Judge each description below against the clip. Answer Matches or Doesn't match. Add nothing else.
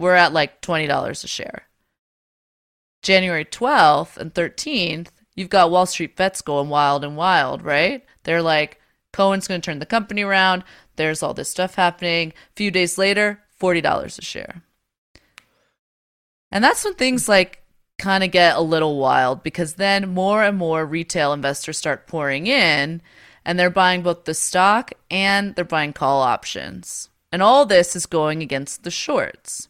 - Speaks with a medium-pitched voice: Matches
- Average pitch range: Matches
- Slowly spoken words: Doesn't match